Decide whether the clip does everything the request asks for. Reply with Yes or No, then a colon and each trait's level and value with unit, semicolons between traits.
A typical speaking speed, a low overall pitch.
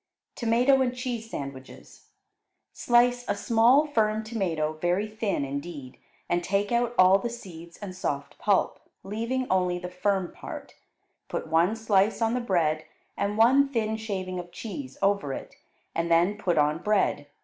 No: average, 155 wpm; high, 200 Hz